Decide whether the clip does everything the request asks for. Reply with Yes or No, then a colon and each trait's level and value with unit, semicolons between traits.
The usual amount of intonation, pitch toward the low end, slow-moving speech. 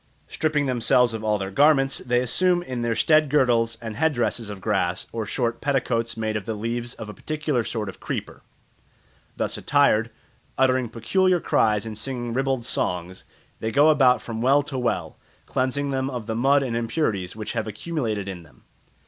No: average, 3.8 semitones; low, 120 Hz; average, 180 wpm